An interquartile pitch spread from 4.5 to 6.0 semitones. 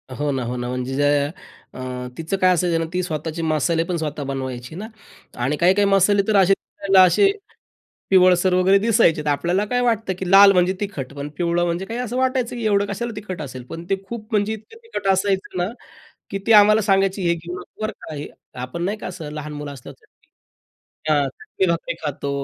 Yes: average, 4.9 semitones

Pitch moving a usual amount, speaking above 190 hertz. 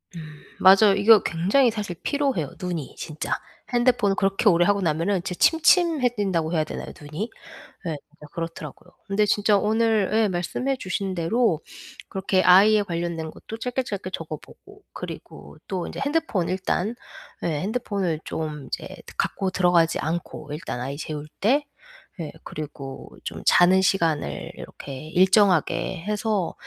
No: average, 4.6 semitones; medium, 185 Hz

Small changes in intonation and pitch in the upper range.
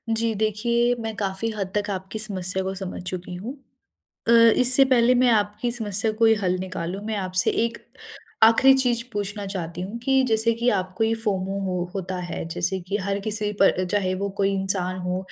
No: average, 3.2 semitones; high, 205 Hz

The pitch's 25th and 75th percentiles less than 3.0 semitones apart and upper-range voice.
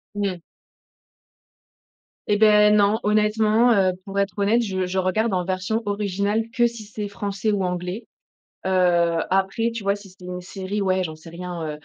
Yes: narrow, 2.4 semitones; high, 200 Hz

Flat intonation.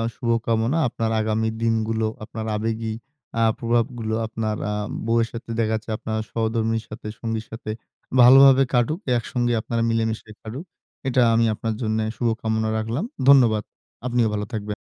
Yes: narrow, 1.2 semitones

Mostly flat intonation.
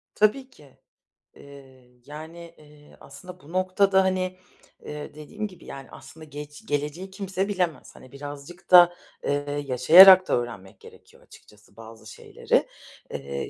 No: average, 4.7 semitones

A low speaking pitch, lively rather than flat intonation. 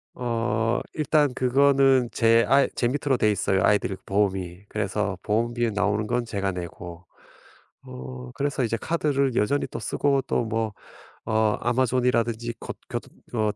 No: low, 115 Hz; average, 3.6 semitones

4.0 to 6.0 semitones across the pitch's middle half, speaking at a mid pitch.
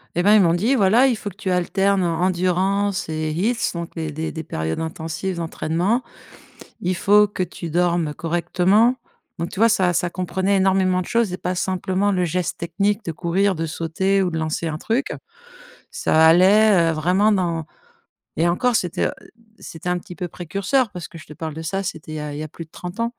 No: average, 3.2 semitones; medium, 180 Hz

